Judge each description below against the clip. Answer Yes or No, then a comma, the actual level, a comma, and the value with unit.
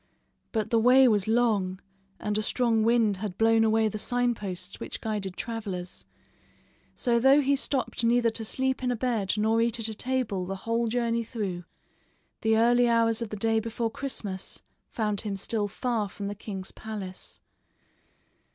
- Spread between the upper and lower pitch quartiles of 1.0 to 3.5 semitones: Yes, narrow, 2.4 semitones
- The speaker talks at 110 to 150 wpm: No, average, 170 wpm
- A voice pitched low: No, high, 225 Hz